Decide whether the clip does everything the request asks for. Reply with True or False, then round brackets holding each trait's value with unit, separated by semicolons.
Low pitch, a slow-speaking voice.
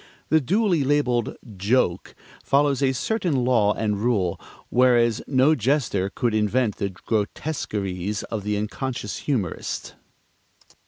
True (120 Hz; 115 wpm)